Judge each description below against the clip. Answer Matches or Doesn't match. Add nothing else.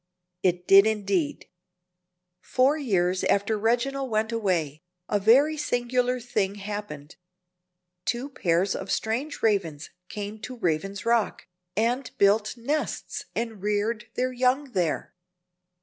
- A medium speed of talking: Doesn't match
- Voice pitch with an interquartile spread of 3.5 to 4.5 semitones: Matches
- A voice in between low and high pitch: Doesn't match